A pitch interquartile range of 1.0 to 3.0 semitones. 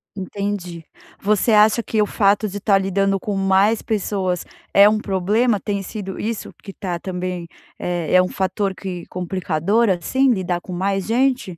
Yes: narrow, 2.4 semitones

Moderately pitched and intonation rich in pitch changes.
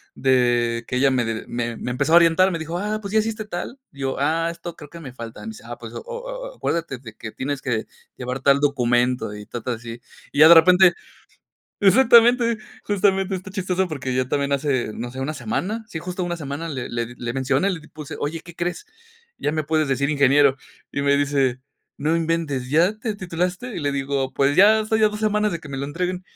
Yes: medium, 155 Hz; wide, 5.9 semitones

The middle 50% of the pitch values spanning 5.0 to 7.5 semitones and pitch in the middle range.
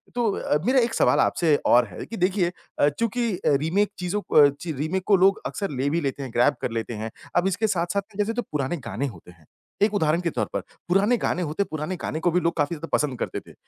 Yes: wide, 5.4 semitones; medium, 175 Hz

